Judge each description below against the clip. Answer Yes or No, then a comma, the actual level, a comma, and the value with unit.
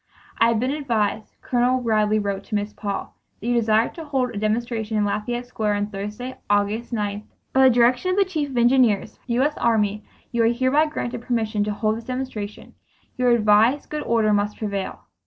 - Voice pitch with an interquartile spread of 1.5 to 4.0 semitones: Yes, average, 3.0 semitones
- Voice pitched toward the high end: Yes, high, 230 Hz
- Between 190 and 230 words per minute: Yes, average, 195 wpm